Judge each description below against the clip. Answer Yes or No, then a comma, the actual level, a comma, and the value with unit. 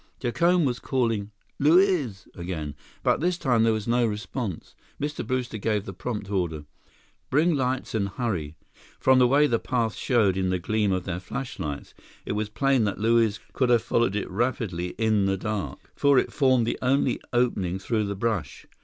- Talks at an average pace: Yes, average, 180 wpm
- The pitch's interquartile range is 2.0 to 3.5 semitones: No, average, 4.8 semitones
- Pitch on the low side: Yes, low, 115 Hz